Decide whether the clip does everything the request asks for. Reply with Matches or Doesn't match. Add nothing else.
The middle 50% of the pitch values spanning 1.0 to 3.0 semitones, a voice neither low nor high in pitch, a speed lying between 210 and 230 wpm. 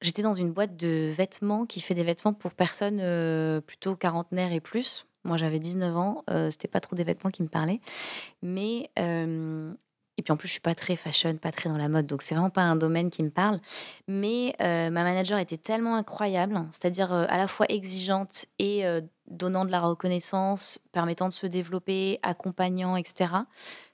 Doesn't match